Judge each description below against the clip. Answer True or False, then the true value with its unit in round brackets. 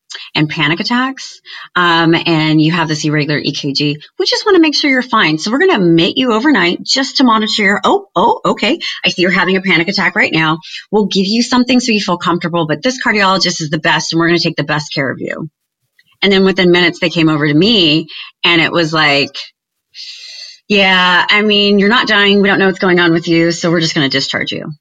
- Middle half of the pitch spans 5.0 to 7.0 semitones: True (5.3 semitones)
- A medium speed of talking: False (240 wpm)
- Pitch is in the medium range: True (175 Hz)